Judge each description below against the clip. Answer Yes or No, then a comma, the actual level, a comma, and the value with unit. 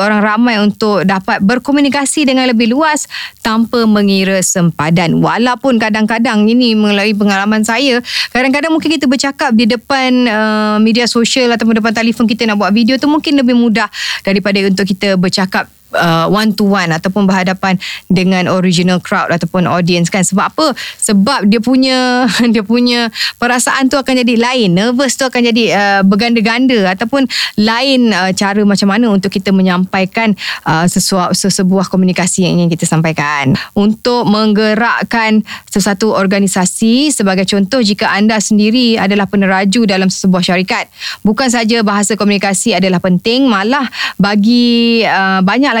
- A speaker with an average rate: No, fast, 145 wpm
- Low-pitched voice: No, high, 215 Hz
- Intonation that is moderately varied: Yes, average, 3.7 semitones